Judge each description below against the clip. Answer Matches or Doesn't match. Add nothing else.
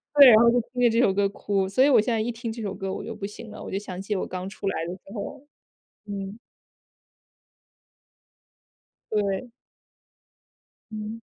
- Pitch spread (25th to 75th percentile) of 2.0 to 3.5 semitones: Matches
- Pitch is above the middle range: Matches